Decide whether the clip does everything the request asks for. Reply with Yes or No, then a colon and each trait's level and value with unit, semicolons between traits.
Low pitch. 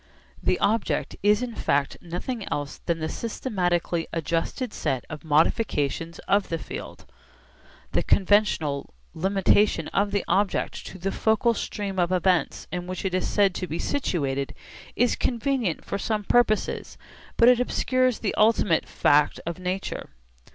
No: high, 190 Hz